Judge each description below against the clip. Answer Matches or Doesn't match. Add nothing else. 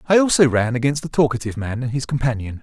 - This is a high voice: Doesn't match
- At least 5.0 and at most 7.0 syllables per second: Matches